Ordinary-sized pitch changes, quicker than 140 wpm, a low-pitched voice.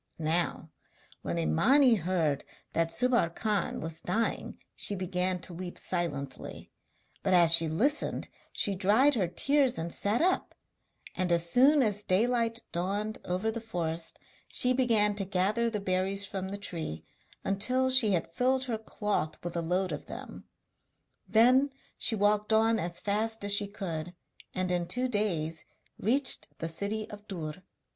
No: average, 4.7 semitones; average, 155 wpm; high, 200 Hz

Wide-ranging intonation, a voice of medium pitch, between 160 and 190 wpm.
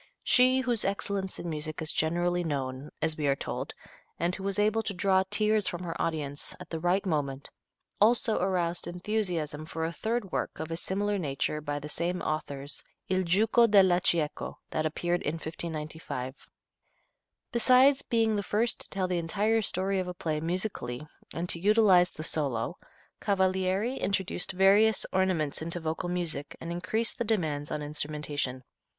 No: average, 4.4 semitones; medium, 175 Hz; average, 165 wpm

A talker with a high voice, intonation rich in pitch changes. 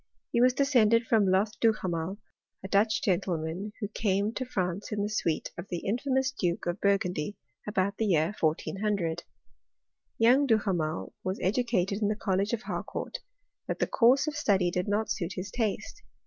No: high, 205 Hz; average, 3.7 semitones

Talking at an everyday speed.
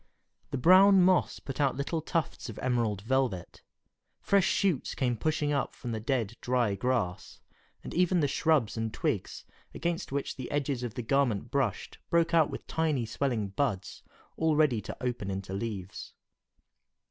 Yes: average, 160 wpm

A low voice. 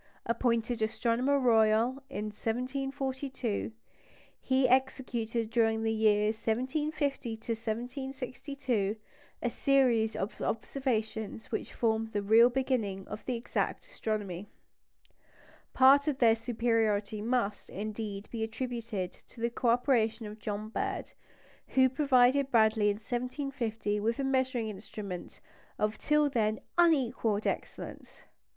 No: high, 230 Hz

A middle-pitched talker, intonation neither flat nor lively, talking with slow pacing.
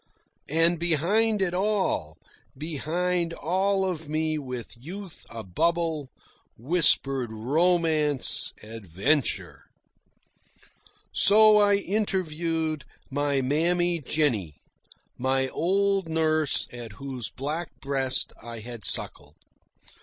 Yes: medium, 155 Hz; average, 5.0 semitones; slow, 90 wpm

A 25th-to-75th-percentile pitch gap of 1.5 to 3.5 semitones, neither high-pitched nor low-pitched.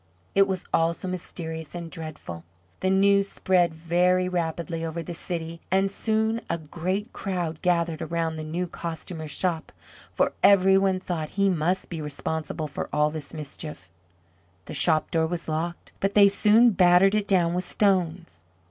Yes: average, 2.9 semitones; medium, 170 Hz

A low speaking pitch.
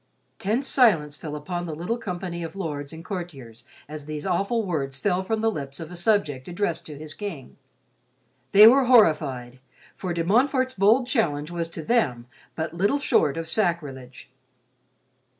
No: medium, 170 Hz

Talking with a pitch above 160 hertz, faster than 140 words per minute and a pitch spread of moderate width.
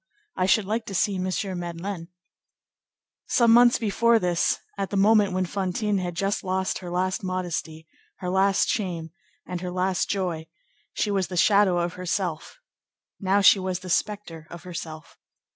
No: medium, 185 Hz; average, 160 wpm; narrow, 2.3 semitones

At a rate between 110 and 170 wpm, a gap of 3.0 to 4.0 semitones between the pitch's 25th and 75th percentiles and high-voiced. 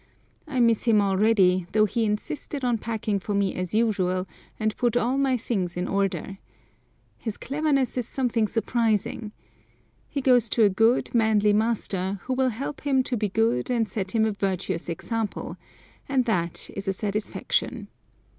Yes: average, 165 wpm; average, 3.6 semitones; high, 220 Hz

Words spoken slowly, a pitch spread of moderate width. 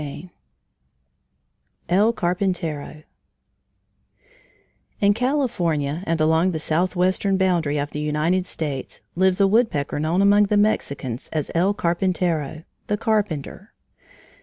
Yes: slow, 110 wpm; average, 4.3 semitones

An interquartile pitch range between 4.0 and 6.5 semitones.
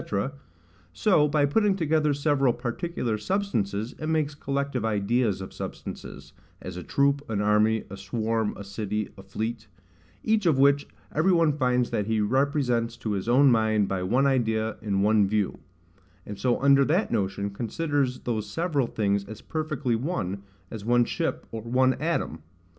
Yes: average, 5.2 semitones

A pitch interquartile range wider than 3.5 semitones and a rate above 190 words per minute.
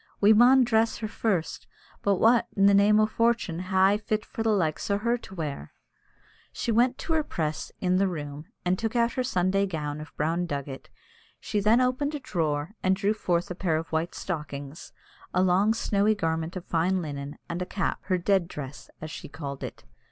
Yes: average, 5.1 semitones; fast, 205 wpm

